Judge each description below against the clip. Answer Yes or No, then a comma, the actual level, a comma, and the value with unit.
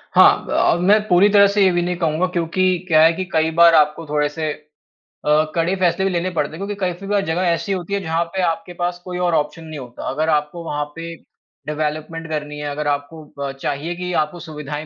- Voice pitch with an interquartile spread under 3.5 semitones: Yes, average, 2.9 semitones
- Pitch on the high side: No, medium, 165 Hz